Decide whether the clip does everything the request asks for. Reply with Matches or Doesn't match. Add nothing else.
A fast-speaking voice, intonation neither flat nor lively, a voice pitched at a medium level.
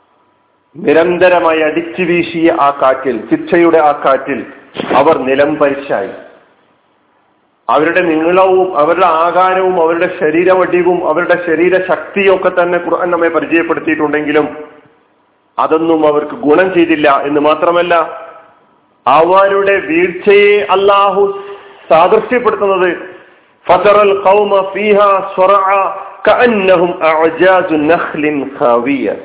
Doesn't match